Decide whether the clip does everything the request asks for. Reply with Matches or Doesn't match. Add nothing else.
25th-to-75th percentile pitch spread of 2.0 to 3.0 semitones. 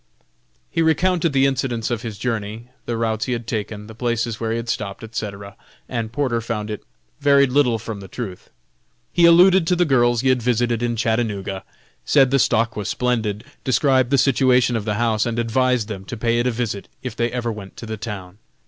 Matches